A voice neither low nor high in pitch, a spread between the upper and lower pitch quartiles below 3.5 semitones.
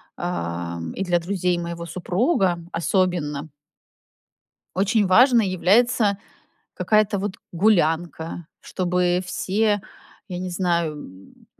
Yes: medium, 180 Hz; average, 2.9 semitones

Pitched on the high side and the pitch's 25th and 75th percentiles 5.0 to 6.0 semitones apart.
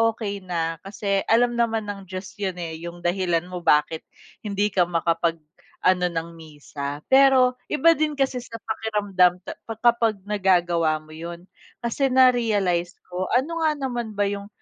Yes: high, 195 Hz; wide, 5.4 semitones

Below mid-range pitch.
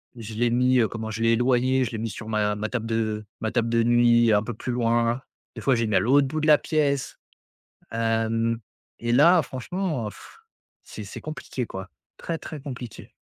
Yes: low, 115 Hz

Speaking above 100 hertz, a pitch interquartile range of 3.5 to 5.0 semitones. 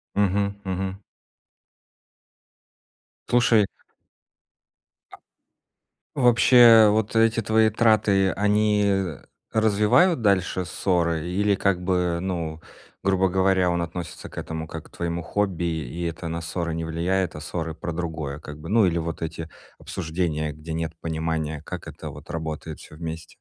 No: very low, 90 Hz; average, 3.8 semitones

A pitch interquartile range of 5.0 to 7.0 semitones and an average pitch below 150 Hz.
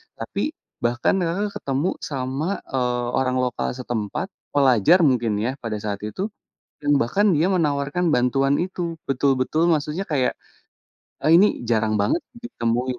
Yes: wide, 5.5 semitones; low, 135 Hz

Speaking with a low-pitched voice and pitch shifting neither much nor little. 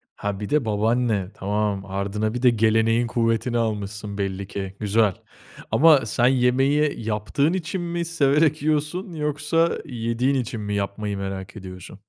No: low, 115 Hz; wide, 5.8 semitones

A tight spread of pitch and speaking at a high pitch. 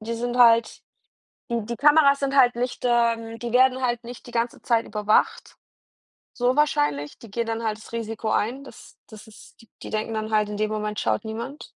Yes: narrow, 2.1 semitones; high, 230 Hz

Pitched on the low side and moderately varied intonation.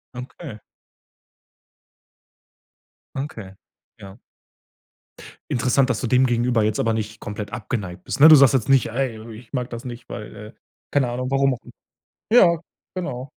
Yes: low, 125 Hz; average, 3.6 semitones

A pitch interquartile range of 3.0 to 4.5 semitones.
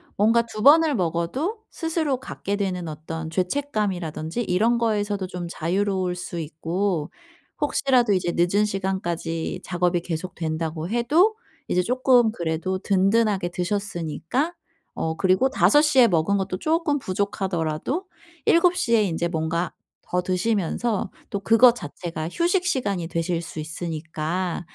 No: wide, 5.6 semitones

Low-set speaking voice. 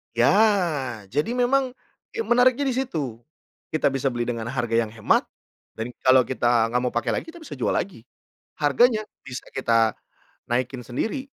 Yes: low, 130 Hz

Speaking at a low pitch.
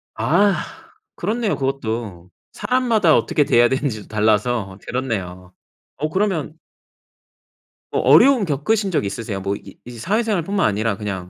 Yes: low, 130 Hz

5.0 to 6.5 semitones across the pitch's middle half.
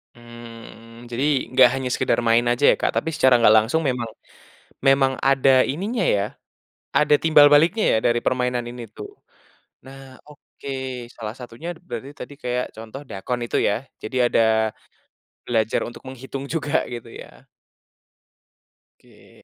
No: average, 2.9 semitones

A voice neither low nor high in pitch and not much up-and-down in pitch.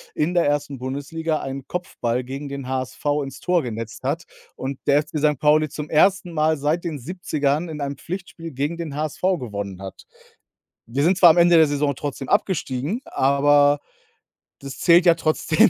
No: medium, 150 Hz; average, 3.3 semitones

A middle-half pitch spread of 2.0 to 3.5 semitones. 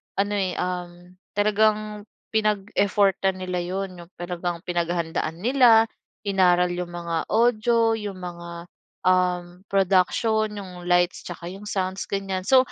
Yes: average, 2.8 semitones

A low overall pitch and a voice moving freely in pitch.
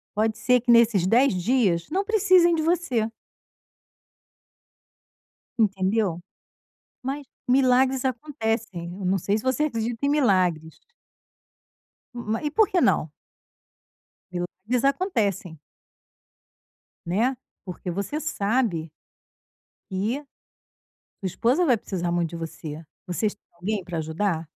No: high, 220 Hz; wide, 6.3 semitones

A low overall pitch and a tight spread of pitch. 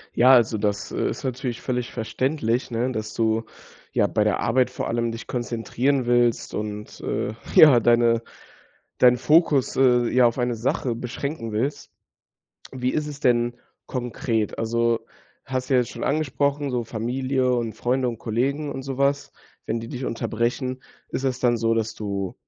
Yes: low, 120 Hz; narrow, 2.3 semitones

